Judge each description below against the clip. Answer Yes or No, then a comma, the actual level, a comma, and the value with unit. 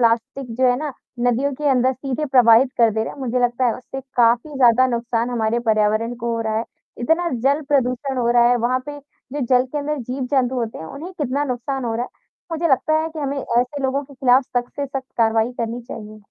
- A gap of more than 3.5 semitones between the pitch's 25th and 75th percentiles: No, average, 2.8 semitones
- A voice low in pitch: No, very high, 250 Hz